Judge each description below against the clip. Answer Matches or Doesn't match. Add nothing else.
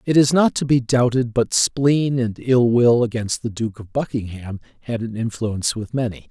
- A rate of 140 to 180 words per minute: Doesn't match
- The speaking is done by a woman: Doesn't match